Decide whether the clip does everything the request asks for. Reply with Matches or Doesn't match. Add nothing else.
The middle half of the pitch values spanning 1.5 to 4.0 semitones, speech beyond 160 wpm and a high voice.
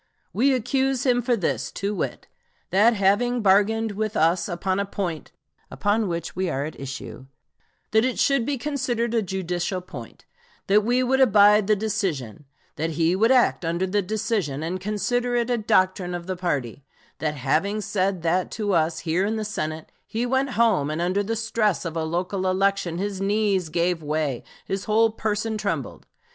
Doesn't match